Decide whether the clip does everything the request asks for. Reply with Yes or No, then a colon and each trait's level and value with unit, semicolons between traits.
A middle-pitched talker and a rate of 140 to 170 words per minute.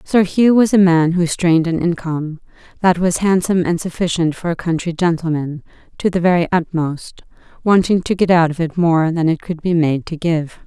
No: medium, 170 Hz; fast, 205 wpm